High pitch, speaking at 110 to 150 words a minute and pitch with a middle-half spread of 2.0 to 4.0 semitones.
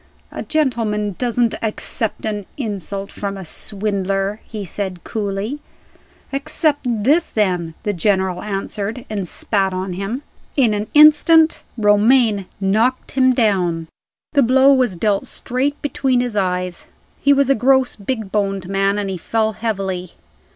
No: high, 210 Hz; average, 140 wpm; average, 4.4 semitones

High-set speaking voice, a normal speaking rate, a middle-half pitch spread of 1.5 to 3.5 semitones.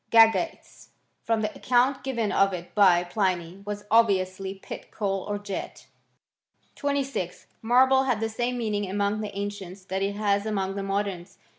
Yes: high, 205 Hz; average, 160 wpm; average, 2.7 semitones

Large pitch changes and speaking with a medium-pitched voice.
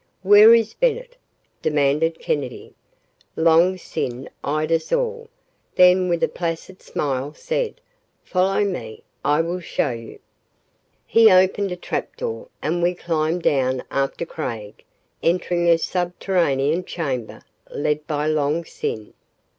No: average, 4.2 semitones; medium, 170 Hz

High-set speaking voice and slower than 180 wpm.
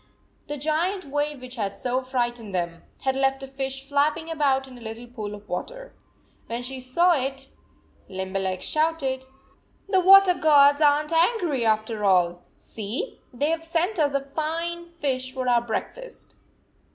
Yes: very high, 270 Hz; average, 160 wpm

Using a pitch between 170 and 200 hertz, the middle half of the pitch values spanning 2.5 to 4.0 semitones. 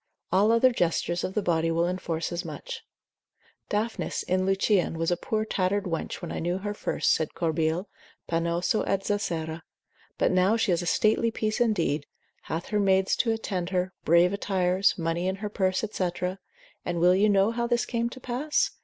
Yes: medium, 185 Hz; average, 3.6 semitones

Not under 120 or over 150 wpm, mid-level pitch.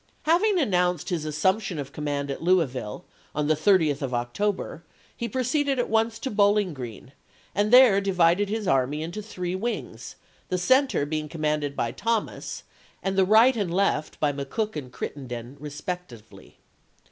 No: average, 160 wpm; medium, 180 Hz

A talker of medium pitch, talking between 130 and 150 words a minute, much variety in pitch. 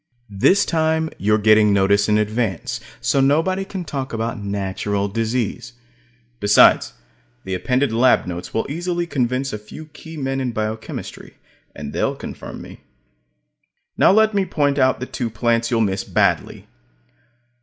No: low, 120 Hz; average, 145 wpm; wide, 5.7 semitones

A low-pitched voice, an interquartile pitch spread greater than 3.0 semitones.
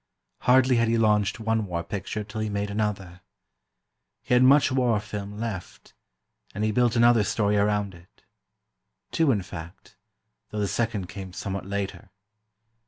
No: low, 105 Hz; narrow, 2.6 semitones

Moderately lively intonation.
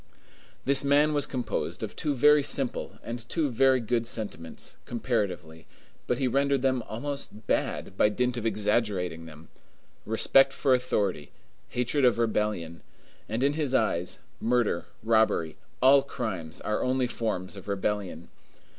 Yes: average, 4.6 semitones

